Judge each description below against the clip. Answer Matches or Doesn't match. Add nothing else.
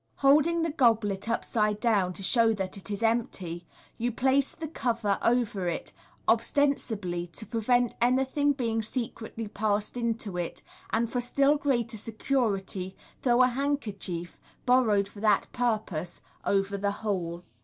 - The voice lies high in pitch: Matches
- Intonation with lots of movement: Doesn't match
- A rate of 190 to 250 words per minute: Doesn't match